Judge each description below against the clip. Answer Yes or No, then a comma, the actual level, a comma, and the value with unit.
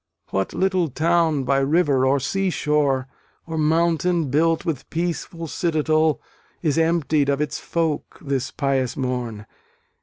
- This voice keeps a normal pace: No, slow, 130 wpm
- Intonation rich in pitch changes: No, average, 3.3 semitones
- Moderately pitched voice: Yes, medium, 155 Hz